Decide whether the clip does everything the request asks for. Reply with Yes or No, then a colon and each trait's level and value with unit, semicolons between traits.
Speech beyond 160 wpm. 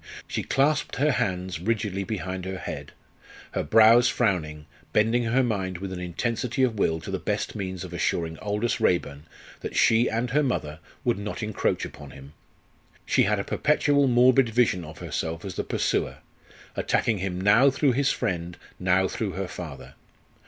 Yes: average, 170 wpm